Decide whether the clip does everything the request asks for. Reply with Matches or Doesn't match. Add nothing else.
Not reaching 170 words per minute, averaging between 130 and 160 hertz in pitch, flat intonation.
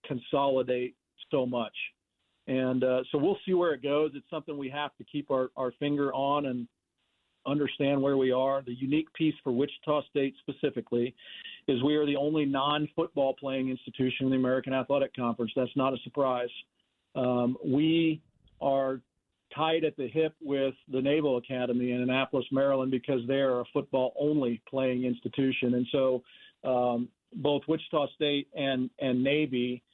Matches